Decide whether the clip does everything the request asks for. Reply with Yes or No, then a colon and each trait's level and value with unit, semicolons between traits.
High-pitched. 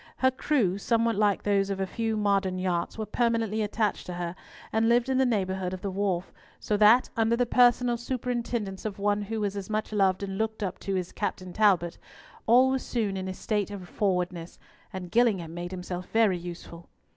Yes: high, 205 Hz